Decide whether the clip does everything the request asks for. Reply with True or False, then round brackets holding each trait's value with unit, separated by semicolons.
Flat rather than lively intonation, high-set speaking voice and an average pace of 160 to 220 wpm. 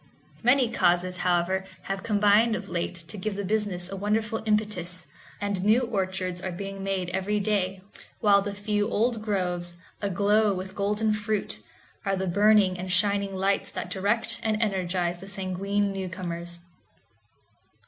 False (2.3 semitones; 195 Hz; 150 wpm)